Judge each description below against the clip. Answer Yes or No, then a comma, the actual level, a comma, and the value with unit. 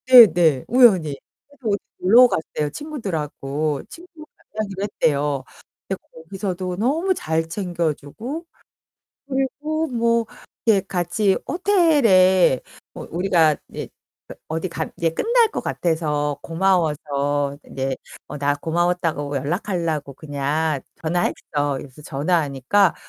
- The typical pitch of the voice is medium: Yes, medium, 175 Hz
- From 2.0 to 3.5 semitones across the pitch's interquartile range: No, wide, 6.7 semitones